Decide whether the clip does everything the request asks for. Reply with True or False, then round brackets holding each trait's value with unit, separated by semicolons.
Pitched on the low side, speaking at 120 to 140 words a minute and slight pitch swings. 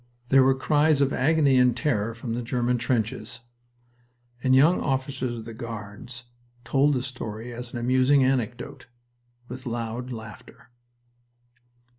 True (125 Hz; 135 wpm; 2.3 semitones)